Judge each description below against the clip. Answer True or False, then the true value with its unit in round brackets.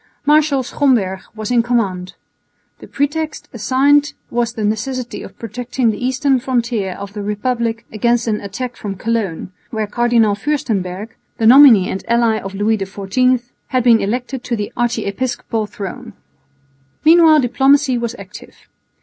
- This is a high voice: True (235 Hz)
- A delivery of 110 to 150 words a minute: True (140 wpm)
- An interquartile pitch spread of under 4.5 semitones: True (3.6 semitones)